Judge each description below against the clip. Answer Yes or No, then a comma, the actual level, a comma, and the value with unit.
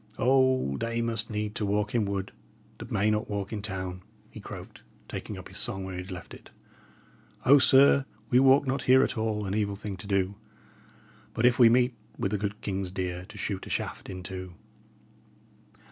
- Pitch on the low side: Yes, low, 105 Hz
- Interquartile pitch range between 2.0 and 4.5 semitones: Yes, average, 3.8 semitones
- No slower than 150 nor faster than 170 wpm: No, average, 195 wpm